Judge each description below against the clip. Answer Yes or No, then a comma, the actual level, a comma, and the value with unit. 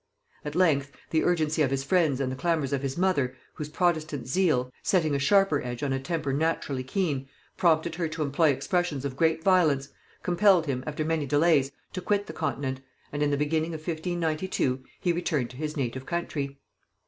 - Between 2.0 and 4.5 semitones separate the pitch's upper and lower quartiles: Yes, average, 3.7 semitones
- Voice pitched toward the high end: No, medium, 155 Hz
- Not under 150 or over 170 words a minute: No, average, 190 wpm